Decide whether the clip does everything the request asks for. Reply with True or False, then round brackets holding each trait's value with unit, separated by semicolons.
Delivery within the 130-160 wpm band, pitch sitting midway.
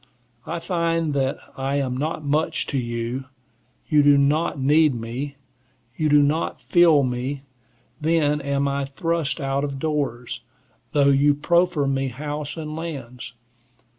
True (140 wpm; 145 Hz)